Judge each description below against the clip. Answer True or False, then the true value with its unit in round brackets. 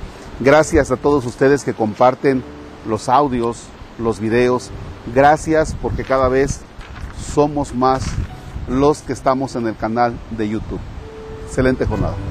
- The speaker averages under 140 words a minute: True (125 wpm)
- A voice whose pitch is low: True (120 Hz)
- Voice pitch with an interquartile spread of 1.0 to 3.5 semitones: False (3.9 semitones)